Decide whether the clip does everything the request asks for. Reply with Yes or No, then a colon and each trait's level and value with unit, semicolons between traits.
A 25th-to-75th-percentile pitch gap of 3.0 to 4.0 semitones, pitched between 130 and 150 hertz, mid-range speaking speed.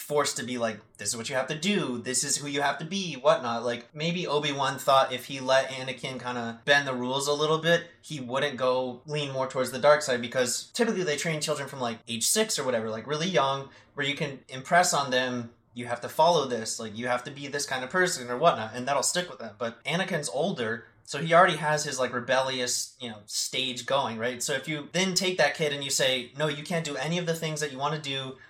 No: average, 3.7 semitones; low, 135 Hz; fast, 260 wpm